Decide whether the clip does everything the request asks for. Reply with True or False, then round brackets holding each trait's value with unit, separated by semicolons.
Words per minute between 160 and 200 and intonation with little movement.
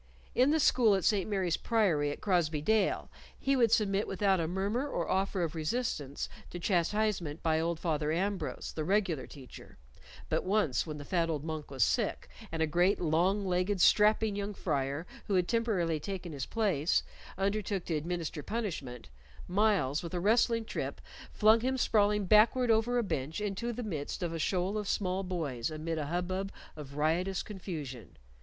False (175 wpm; 4.8 semitones)